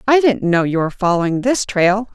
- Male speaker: No, female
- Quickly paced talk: Yes, fast, 225 wpm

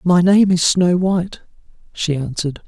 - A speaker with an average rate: Yes, average, 155 wpm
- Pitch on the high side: No, medium, 175 Hz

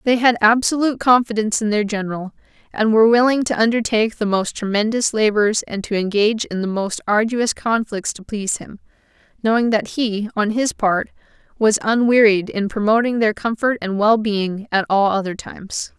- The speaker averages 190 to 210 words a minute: No, average, 175 wpm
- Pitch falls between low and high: No, high, 220 Hz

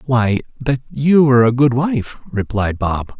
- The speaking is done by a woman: No, male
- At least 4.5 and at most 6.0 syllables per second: No, 4.2 syllables/s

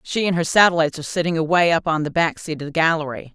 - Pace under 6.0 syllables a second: No, 7.1 syllables/s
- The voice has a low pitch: No, medium, 165 Hz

